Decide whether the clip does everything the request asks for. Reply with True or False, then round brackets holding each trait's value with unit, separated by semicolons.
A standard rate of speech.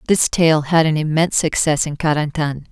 True (175 wpm)